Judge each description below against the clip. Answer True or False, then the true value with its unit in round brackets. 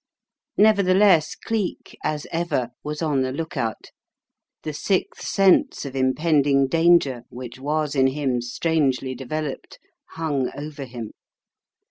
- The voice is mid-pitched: True (145 Hz)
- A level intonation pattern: False (3.9 semitones)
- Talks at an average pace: False (120 wpm)